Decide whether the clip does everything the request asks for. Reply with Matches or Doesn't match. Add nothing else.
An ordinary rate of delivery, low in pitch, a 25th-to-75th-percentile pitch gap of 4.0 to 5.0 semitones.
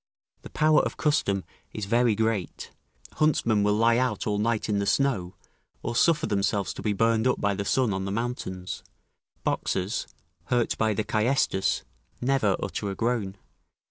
Doesn't match